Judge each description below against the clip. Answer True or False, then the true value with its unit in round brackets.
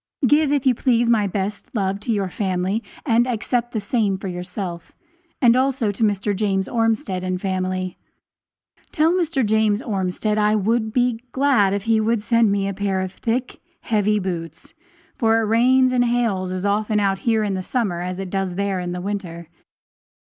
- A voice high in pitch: True (210 Hz)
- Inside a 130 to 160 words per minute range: False (180 wpm)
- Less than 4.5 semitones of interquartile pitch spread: True (3.5 semitones)